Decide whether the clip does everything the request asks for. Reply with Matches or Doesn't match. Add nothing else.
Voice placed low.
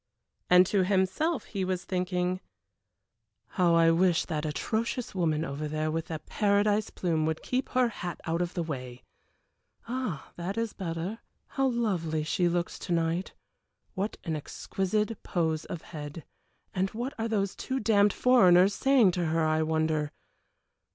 Doesn't match